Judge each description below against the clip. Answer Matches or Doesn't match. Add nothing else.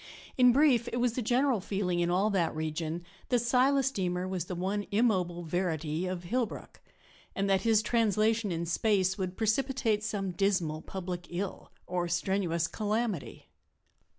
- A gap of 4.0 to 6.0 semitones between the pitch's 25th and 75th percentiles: Matches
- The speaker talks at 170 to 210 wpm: Doesn't match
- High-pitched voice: Matches